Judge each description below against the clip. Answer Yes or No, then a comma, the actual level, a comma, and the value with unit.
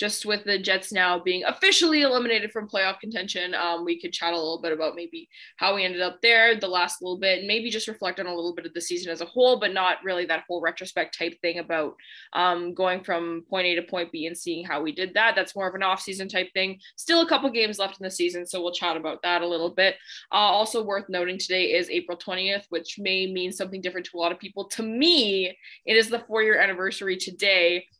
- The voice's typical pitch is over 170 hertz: Yes, medium, 185 Hz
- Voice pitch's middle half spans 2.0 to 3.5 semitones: Yes, narrow, 2.6 semitones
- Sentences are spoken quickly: Yes, fast, 250 wpm